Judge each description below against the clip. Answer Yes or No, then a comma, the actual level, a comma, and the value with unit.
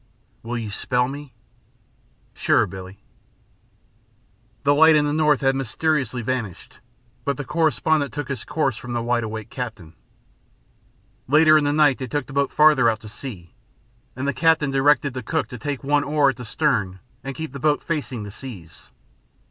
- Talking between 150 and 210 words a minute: Yes, average, 175 wpm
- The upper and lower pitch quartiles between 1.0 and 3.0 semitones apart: No, average, 3.9 semitones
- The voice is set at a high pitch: No, low, 135 Hz